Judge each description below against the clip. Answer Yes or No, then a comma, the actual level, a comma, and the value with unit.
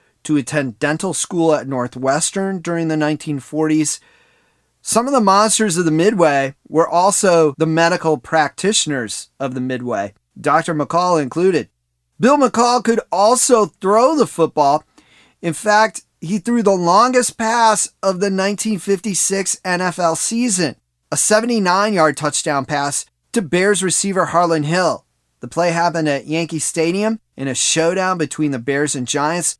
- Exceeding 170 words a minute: No, average, 140 wpm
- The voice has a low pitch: No, medium, 170 Hz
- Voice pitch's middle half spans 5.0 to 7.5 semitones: Yes, wide, 5.4 semitones